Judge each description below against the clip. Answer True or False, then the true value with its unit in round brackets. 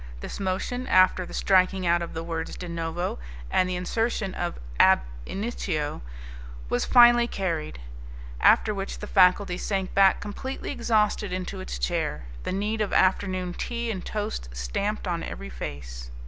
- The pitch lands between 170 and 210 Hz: True (185 Hz)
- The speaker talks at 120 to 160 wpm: True (155 wpm)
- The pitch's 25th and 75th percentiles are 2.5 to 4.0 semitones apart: True (3.6 semitones)